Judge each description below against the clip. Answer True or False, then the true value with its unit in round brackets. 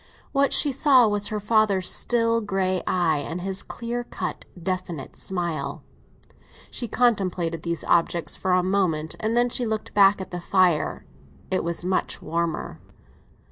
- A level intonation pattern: False (4.1 semitones)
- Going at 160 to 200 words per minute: False (150 wpm)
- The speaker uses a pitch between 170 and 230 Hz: True (190 Hz)